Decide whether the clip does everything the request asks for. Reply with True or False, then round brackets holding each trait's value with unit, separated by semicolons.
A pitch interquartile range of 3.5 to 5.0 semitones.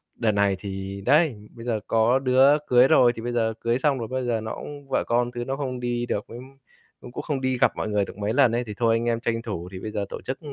False (2.8 semitones)